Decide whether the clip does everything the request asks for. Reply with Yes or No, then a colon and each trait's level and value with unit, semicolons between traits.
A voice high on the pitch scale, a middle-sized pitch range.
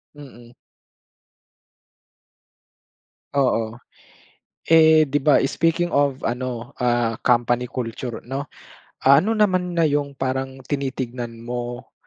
No: low, 130 Hz; average, 3.3 semitones